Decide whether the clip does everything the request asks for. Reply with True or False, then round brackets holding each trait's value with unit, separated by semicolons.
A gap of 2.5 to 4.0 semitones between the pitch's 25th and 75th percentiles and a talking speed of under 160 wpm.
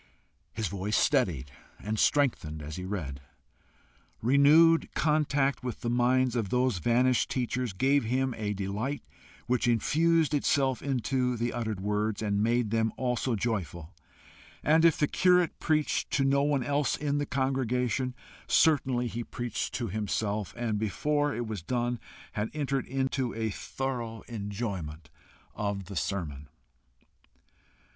False (4.6 semitones; 135 wpm)